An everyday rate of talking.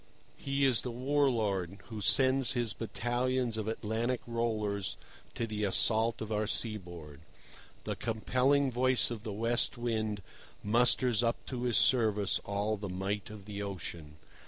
Yes: average, 150 wpm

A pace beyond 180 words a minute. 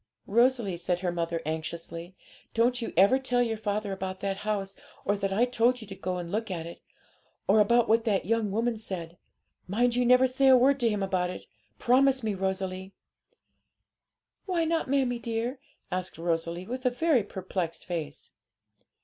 No: average, 175 wpm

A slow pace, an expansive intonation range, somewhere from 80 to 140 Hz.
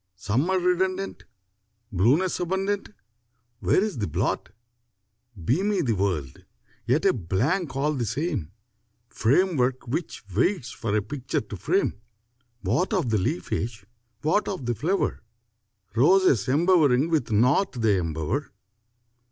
Yes: slow, 120 wpm; wide, 8.5 semitones; low, 135 Hz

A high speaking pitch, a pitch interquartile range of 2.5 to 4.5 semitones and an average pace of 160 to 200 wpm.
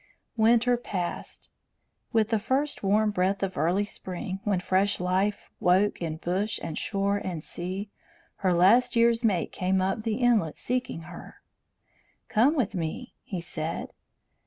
No: high, 200 Hz; average, 3.6 semitones; average, 145 wpm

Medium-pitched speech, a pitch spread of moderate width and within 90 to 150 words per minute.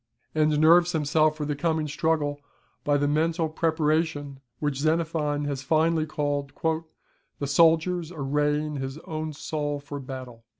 No: medium, 150 Hz; narrow, 1.8 semitones; average, 140 wpm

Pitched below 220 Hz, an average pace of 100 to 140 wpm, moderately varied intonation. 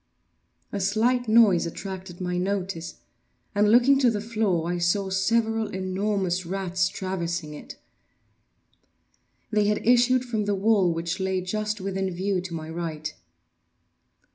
Yes: high, 190 Hz; slow, 135 wpm; average, 3.0 semitones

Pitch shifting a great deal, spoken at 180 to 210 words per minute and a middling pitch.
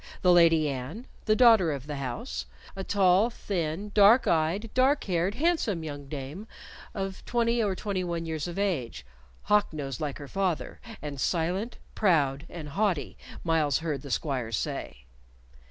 No: wide, 5.9 semitones; average, 155 wpm; medium, 170 Hz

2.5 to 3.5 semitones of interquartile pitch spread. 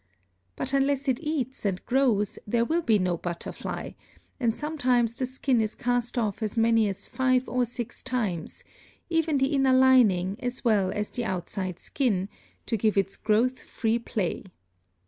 No: average, 4.0 semitones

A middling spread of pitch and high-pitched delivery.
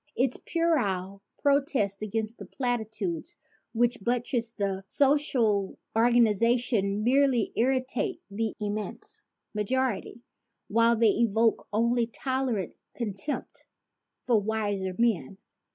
Yes: average, 3.3 semitones; high, 230 Hz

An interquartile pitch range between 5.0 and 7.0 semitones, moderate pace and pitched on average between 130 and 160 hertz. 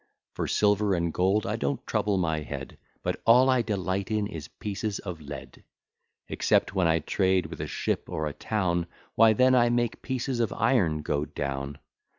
No: wide, 5.5 semitones; average, 180 wpm; very low, 95 Hz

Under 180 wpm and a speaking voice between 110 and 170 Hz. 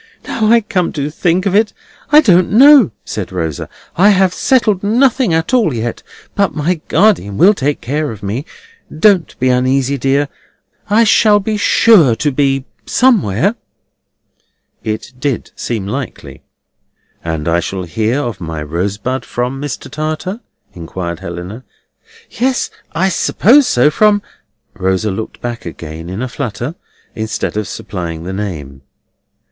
Yes: average, 145 wpm; low, 135 Hz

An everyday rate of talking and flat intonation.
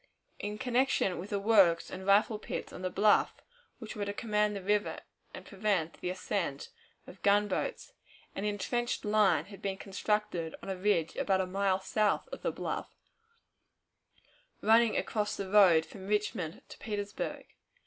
Yes: average, 160 wpm; narrow, 2.0 semitones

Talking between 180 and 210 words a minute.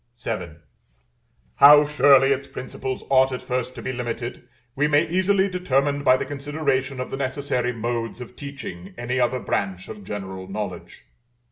No: average, 155 wpm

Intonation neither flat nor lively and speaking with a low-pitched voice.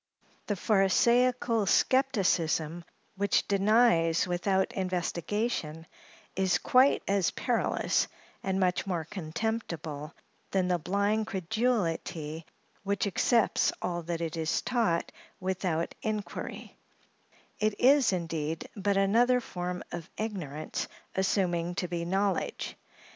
No: average, 4.0 semitones; high, 190 Hz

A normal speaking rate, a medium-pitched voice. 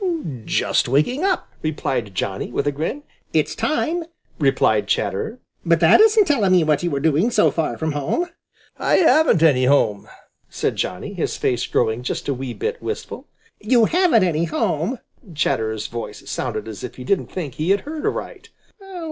Yes: average, 175 wpm; medium, 155 Hz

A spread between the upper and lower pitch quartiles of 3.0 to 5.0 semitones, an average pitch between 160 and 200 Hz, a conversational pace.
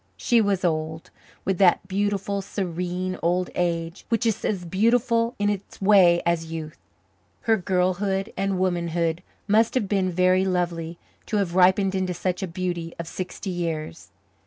No: narrow, 2.5 semitones; medium, 185 Hz; average, 155 wpm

